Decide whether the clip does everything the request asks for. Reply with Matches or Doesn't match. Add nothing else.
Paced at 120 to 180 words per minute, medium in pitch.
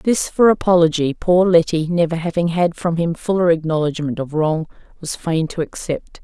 Matches